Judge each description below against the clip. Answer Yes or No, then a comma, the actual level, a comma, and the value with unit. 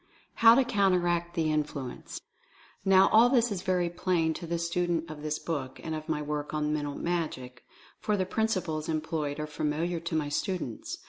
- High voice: No, medium, 165 Hz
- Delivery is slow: No, average, 180 wpm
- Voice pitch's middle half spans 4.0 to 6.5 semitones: No, average, 3.2 semitones